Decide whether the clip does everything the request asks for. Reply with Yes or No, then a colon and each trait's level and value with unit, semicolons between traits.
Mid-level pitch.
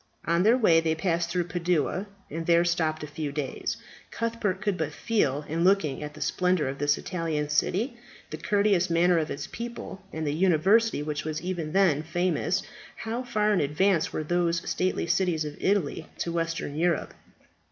Yes: medium, 170 Hz